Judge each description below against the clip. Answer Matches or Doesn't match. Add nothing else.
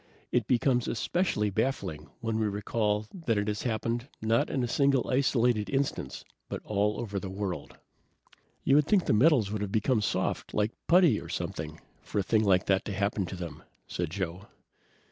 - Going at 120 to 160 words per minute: Doesn't match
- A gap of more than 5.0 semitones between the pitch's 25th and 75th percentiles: Doesn't match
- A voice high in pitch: Doesn't match